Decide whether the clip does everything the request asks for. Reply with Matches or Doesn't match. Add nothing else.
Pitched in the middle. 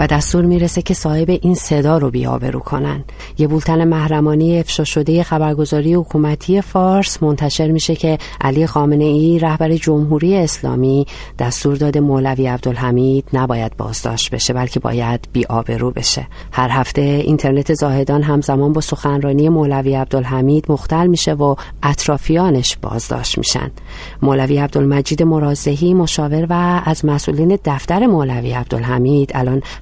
Matches